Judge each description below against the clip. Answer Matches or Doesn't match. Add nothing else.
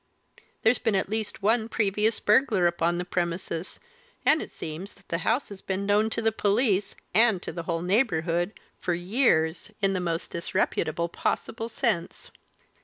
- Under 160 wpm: Doesn't match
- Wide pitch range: Doesn't match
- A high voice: Matches